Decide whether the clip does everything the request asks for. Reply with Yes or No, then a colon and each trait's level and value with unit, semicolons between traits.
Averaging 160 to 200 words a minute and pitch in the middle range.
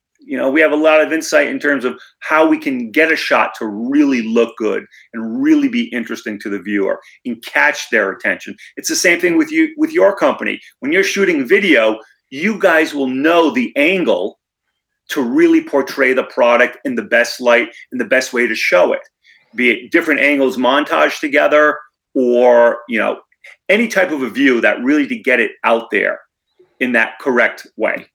Yes: average, 195 wpm; medium, 160 Hz